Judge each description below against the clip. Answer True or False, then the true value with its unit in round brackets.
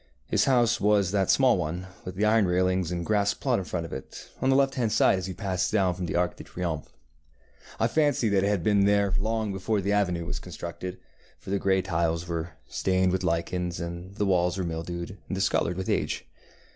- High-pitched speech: False (95 Hz)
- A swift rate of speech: True (220 wpm)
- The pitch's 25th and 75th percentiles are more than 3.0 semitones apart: False (2.7 semitones)